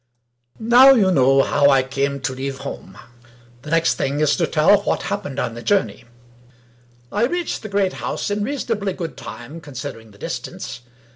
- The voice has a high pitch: No, medium, 155 Hz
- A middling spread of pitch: No, wide, 7.1 semitones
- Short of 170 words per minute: No, average, 180 wpm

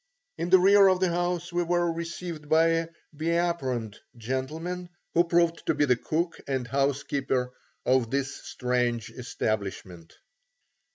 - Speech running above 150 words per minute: No, average, 145 wpm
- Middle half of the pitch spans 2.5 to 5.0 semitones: No, wide, 5.5 semitones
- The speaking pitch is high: No, medium, 155 Hz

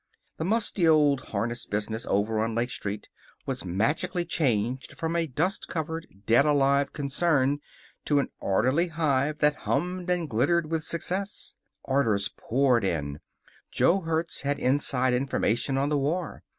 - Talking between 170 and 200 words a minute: No, average, 145 wpm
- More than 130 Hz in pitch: Yes, medium, 140 Hz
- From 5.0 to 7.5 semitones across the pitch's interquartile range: Yes, average, 5.3 semitones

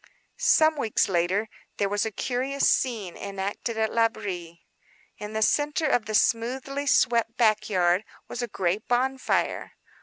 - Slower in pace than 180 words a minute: Yes, average, 145 wpm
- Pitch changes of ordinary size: Yes, average, 3.9 semitones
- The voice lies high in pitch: Yes, high, 220 Hz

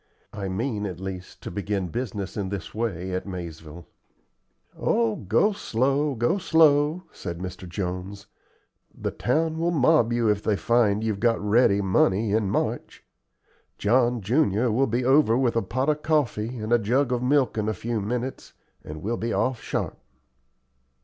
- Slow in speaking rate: No, average, 165 wpm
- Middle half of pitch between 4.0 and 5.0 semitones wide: Yes, average, 4.5 semitones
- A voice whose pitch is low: Yes, low, 110 Hz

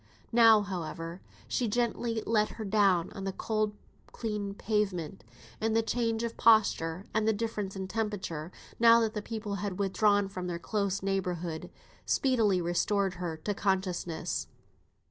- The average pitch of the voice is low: No, high, 205 Hz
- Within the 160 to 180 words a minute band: No, average, 145 wpm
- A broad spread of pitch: No, average, 3.1 semitones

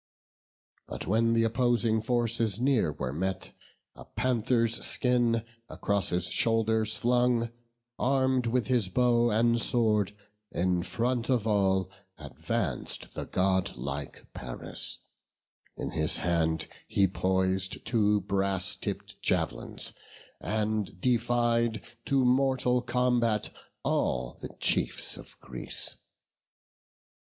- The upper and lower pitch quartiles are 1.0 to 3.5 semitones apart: No, average, 4.2 semitones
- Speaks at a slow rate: Yes, slow, 105 wpm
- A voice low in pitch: Yes, low, 110 Hz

